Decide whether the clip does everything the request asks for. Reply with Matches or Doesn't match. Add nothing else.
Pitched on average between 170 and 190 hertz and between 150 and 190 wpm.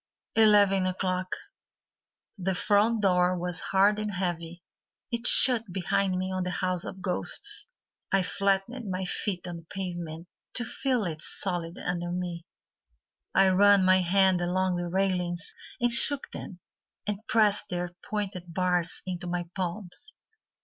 Doesn't match